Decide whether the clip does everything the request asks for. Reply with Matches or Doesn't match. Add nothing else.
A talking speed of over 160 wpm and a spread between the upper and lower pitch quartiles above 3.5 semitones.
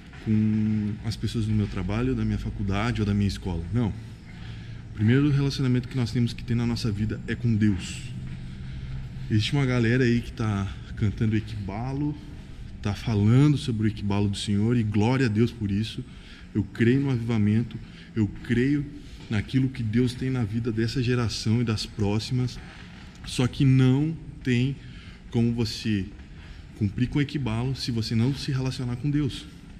Doesn't match